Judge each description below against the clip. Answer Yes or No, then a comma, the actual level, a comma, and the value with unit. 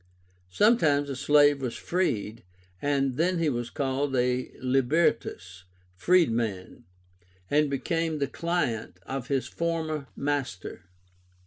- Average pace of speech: No, slow, 110 wpm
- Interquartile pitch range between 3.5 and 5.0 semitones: Yes, average, 4.2 semitones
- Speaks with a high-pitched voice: No, medium, 140 Hz